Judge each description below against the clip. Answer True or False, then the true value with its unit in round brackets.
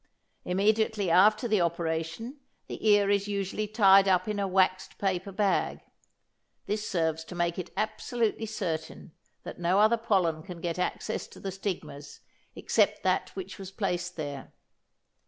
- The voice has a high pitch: True (195 Hz)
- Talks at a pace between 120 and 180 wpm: True (150 wpm)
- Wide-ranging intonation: False (3.4 semitones)